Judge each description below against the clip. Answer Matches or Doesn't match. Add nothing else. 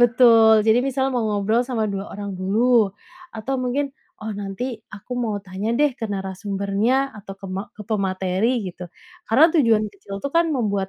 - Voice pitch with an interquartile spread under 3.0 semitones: Doesn't match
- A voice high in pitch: Matches